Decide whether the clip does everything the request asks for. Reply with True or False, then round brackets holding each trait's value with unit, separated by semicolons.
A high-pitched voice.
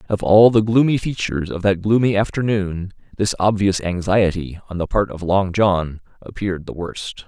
False (100 Hz)